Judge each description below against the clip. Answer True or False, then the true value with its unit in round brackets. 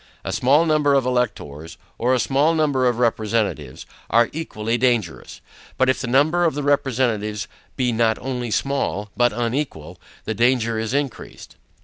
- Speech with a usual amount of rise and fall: True (3.7 semitones)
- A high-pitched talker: False (125 Hz)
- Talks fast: False (155 wpm)